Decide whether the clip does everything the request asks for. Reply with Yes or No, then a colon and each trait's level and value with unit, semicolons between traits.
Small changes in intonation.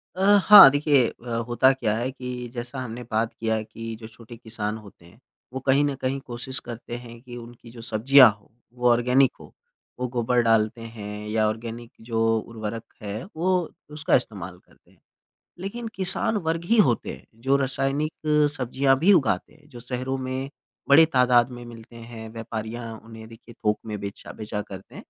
No: average, 3.0 semitones